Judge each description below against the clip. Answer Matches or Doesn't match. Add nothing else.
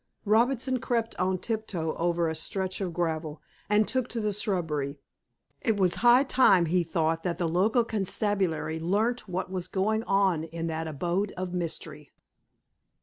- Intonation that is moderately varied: Matches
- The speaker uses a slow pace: Doesn't match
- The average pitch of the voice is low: Doesn't match